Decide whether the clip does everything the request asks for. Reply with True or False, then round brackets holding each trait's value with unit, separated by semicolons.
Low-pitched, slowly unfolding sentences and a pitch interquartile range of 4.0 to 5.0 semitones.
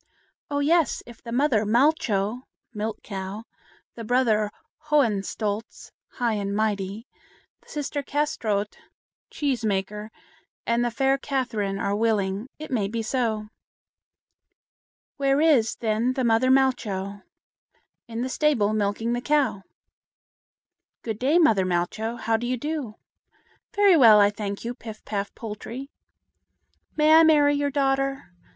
False (230 Hz; 130 wpm; 4.5 semitones)